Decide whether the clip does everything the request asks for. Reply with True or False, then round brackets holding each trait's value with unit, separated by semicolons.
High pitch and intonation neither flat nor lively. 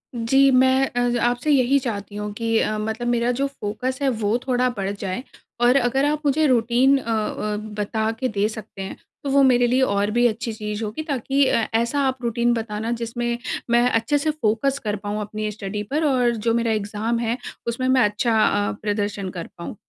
True (235 Hz; 3.2 semitones)